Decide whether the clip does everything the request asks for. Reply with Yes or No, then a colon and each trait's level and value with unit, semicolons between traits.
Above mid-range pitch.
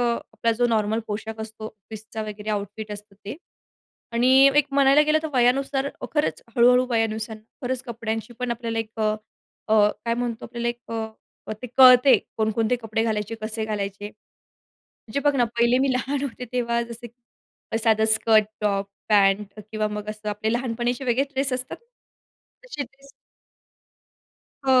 Yes: high, 230 Hz